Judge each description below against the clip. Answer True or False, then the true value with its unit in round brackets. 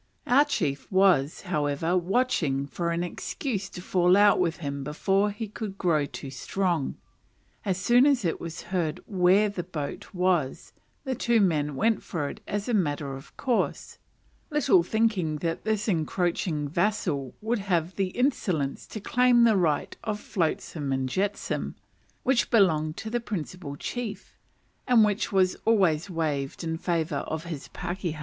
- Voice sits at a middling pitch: True (180 Hz)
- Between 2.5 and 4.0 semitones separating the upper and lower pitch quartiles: False (5.1 semitones)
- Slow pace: False (155 wpm)